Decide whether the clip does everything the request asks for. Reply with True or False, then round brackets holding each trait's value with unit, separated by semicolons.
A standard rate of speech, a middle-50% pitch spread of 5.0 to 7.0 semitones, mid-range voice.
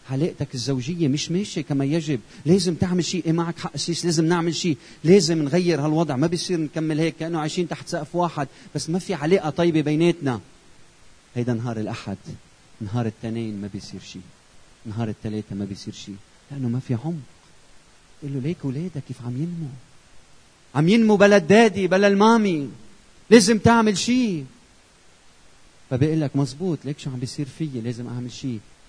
False (160 wpm; 5.5 semitones; 150 Hz)